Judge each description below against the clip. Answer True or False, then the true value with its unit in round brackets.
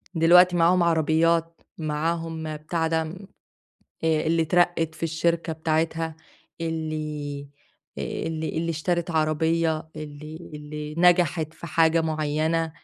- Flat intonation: True (1.2 semitones)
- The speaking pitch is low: False (160 Hz)